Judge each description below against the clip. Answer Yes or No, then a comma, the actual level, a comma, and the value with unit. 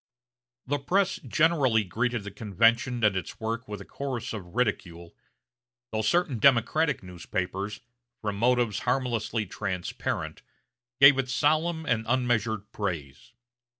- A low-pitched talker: Yes, low, 115 Hz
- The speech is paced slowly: Yes, slow, 120 wpm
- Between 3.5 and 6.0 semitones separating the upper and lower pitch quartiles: Yes, average, 4.2 semitones